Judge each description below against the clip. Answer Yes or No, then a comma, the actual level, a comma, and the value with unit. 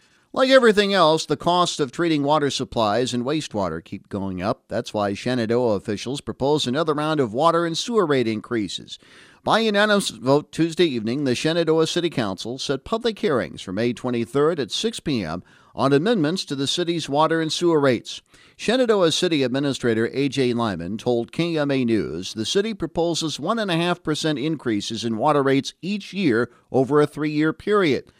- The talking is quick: No, average, 170 wpm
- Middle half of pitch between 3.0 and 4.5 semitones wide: No, wide, 5.6 semitones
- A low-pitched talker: No, medium, 150 Hz